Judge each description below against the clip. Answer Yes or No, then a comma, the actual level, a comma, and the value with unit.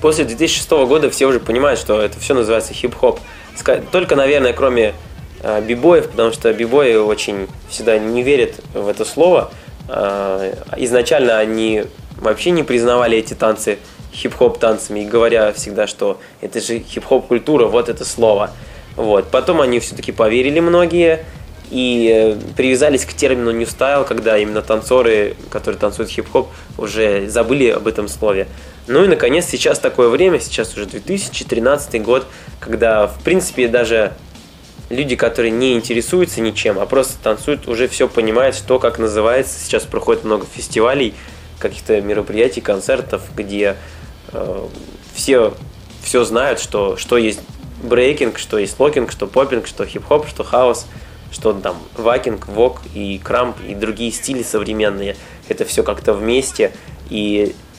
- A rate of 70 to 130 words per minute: No, average, 140 wpm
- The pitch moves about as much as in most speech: No, wide, 6.0 semitones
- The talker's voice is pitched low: Yes, low, 120 Hz